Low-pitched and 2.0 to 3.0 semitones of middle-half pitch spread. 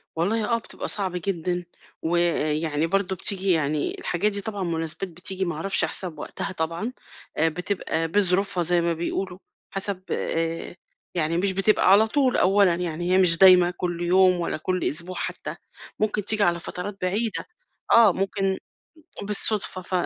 No: medium, 185 Hz; average, 2.7 semitones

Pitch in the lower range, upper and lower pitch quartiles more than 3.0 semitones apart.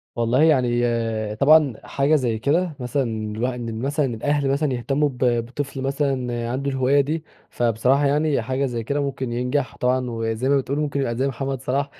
No: low, 130 Hz; average, 2.7 semitones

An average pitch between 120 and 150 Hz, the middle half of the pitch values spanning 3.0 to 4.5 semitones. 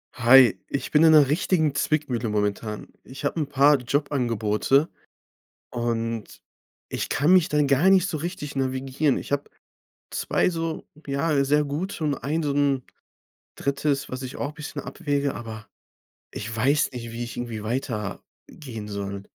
Yes: medium, 140 Hz; average, 4.1 semitones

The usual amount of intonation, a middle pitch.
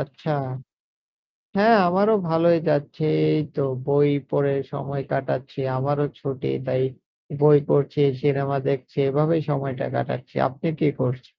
No: narrow, 2.0 semitones; medium, 145 Hz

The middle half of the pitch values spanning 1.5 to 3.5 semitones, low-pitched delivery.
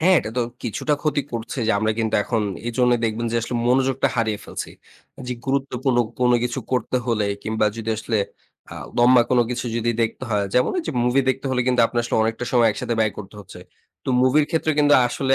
Yes: narrow, 2.5 semitones; low, 120 Hz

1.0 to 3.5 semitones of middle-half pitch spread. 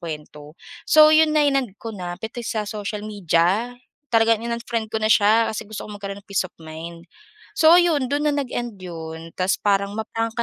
No: average, 4.4 semitones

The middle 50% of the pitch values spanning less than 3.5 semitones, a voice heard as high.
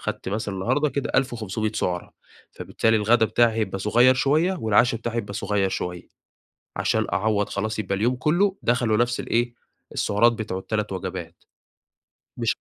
No: average, 3.1 semitones; low, 110 Hz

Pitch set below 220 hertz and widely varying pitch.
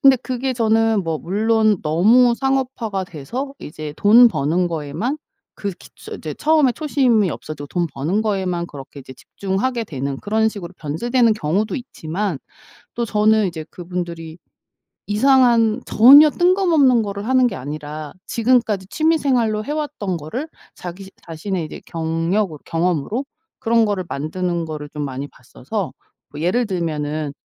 Yes: high, 200 Hz; wide, 6.8 semitones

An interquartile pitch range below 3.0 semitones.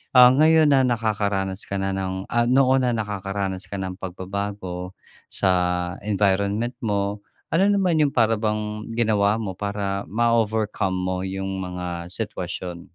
No: average, 3.3 semitones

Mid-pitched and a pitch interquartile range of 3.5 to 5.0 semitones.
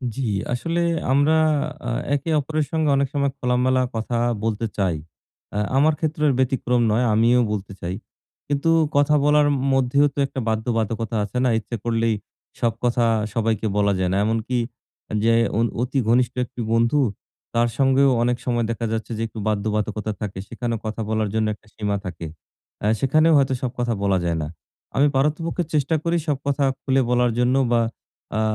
No: low, 120 Hz; average, 3.9 semitones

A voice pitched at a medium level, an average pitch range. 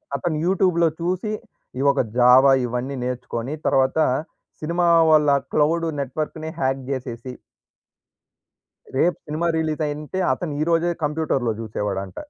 Yes: medium, 150 Hz; average, 4.4 semitones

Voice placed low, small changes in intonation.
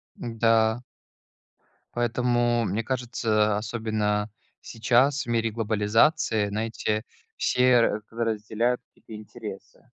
Yes: low, 115 Hz; narrow, 1.9 semitones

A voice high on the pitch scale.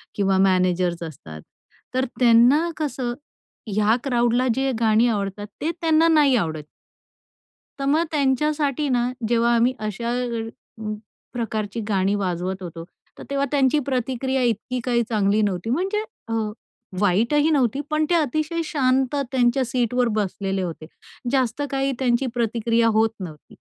Yes: high, 240 Hz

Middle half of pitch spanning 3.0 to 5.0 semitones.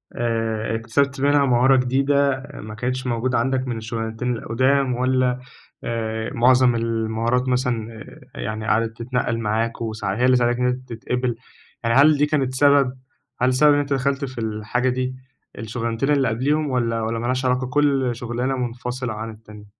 No: narrow, 2.4 semitones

